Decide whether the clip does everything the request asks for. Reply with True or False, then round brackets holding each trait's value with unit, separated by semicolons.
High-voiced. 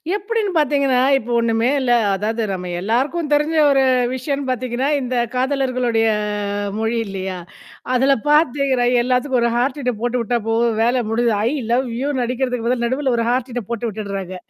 True (250 Hz)